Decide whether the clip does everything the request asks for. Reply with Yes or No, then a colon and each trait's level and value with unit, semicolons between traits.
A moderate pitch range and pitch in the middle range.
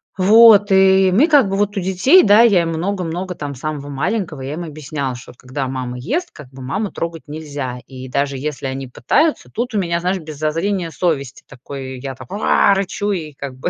No: wide, 6.2 semitones; medium, 165 Hz